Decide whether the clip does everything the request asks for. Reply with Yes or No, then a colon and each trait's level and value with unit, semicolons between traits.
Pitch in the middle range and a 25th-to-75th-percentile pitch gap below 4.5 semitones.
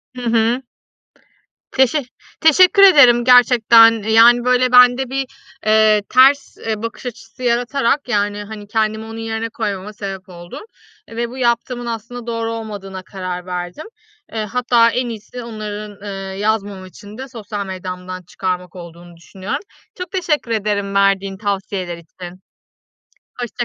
No: high, 220 Hz; average, 3.7 semitones